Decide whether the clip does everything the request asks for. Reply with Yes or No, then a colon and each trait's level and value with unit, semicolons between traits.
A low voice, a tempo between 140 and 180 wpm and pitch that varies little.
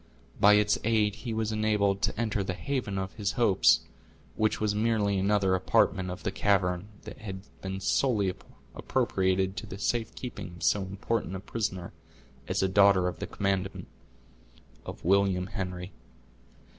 Yes: low, 100 Hz; average, 155 wpm; narrow, 2.1 semitones